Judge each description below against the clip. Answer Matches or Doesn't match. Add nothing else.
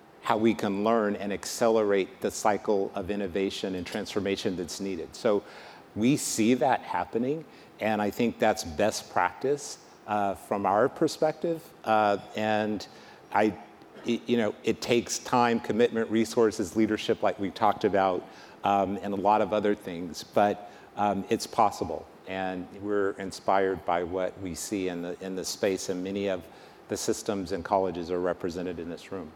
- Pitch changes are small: Matches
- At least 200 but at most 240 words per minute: Doesn't match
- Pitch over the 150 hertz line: Doesn't match